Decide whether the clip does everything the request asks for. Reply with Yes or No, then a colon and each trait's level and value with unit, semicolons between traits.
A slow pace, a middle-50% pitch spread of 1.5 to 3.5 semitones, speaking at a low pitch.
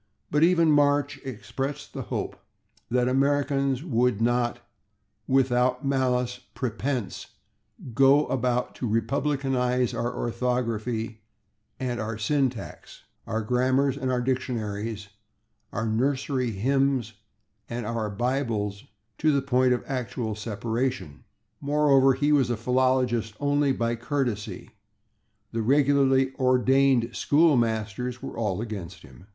Yes: slow, 115 wpm; average, 2.9 semitones; low, 125 Hz